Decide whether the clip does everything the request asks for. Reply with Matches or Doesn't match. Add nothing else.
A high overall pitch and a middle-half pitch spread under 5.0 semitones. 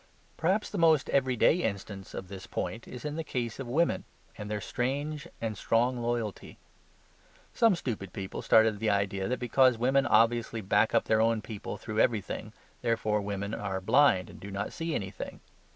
Doesn't match